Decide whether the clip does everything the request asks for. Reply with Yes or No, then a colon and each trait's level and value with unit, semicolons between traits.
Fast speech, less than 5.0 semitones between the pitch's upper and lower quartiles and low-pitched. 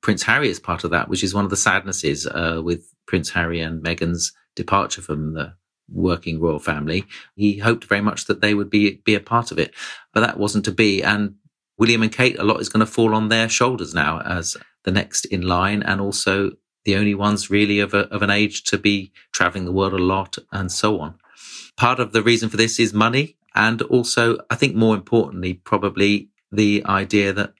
Yes: fast, 215 wpm; average, 2.8 semitones; low, 100 Hz